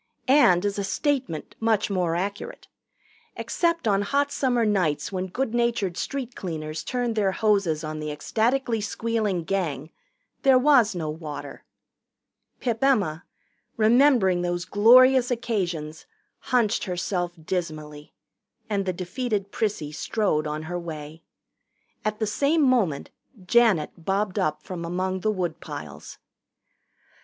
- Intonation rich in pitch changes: Yes, wide, 5.9 semitones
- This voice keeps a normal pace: No, slow, 125 wpm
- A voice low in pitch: No, high, 195 Hz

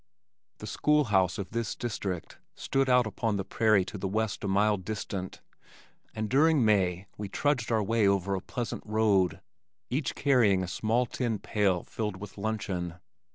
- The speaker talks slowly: No, average, 165 wpm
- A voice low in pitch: Yes, low, 105 Hz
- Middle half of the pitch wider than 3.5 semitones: No, average, 3.1 semitones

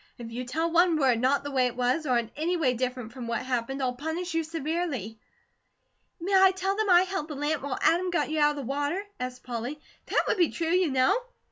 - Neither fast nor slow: No, fast, 240 wpm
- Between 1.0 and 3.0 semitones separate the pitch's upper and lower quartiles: No, average, 5.2 semitones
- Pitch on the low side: No, very high, 290 Hz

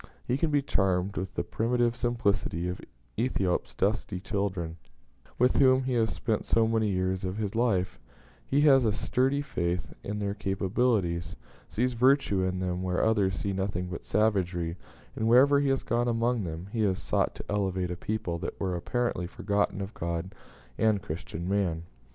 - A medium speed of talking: Yes, average, 175 wpm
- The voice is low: Yes, low, 100 Hz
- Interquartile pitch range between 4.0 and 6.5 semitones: Yes, average, 4.5 semitones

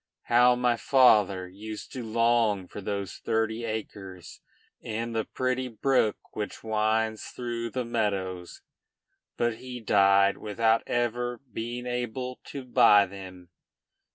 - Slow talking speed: Yes, slow, 125 wpm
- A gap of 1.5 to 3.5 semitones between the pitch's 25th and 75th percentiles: Yes, average, 3.0 semitones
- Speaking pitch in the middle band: No, low, 110 Hz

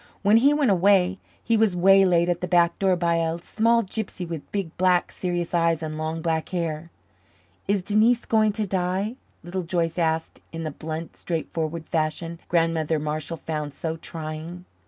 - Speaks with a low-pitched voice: No, medium, 170 Hz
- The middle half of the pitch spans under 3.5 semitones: Yes, average, 3.0 semitones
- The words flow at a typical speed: Yes, average, 170 wpm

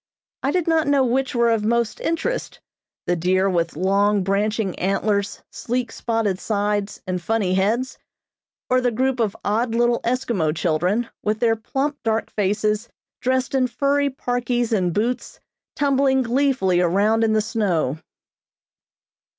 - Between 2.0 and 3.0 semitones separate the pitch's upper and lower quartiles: No, average, 4.2 semitones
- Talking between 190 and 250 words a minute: No, average, 140 wpm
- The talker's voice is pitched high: Yes, high, 225 Hz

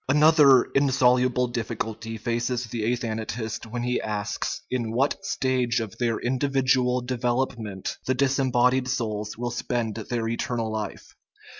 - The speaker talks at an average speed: No, slow, 130 wpm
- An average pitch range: No, narrow, 2.2 semitones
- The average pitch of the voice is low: Yes, low, 120 Hz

